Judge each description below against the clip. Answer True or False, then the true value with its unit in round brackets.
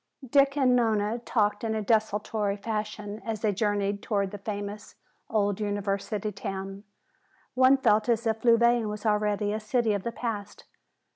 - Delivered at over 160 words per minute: False (155 wpm)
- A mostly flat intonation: True (1.9 semitones)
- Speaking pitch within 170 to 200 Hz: False (210 Hz)